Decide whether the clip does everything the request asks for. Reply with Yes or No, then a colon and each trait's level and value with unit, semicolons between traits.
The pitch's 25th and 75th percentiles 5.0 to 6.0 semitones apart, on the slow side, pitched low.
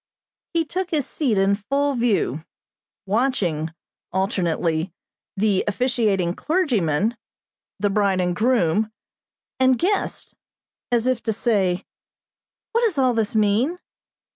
No: average, 5.3 semitones; slow, 115 wpm; high, 215 Hz